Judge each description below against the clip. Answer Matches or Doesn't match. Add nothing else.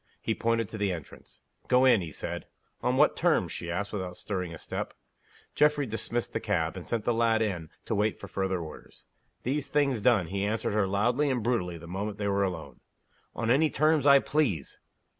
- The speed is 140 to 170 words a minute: Doesn't match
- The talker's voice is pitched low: Matches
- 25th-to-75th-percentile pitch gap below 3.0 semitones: Doesn't match